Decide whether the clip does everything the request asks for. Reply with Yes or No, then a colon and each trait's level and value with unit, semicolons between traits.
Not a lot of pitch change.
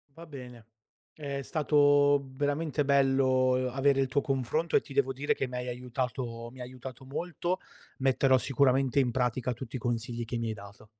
Yes: narrow, 2.2 semitones